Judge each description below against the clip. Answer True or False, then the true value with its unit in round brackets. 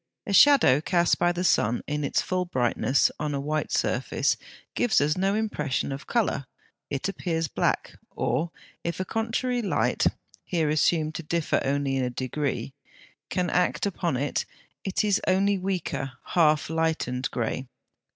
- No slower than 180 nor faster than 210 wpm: False (150 wpm)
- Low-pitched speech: False (160 Hz)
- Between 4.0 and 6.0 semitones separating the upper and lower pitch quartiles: True (5.0 semitones)